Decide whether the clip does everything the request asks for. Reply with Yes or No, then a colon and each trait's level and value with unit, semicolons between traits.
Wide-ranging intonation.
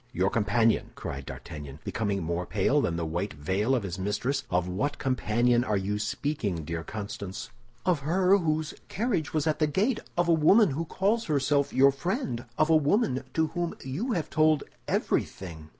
Yes: wide, 8.4 semitones